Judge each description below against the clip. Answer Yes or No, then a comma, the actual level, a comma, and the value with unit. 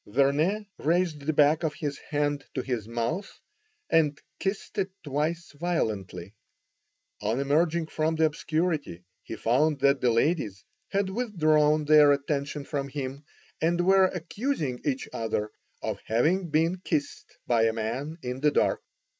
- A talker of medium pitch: Yes, medium, 150 Hz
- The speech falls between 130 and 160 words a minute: Yes, average, 145 wpm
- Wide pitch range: No, average, 4.0 semitones